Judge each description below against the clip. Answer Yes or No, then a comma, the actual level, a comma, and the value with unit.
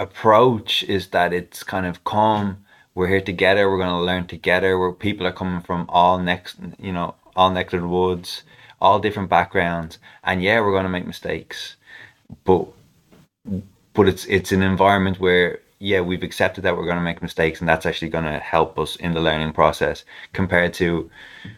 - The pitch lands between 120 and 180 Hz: No, very low, 90 Hz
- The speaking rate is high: No, average, 185 wpm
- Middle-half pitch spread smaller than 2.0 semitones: Yes, narrow, 1.6 semitones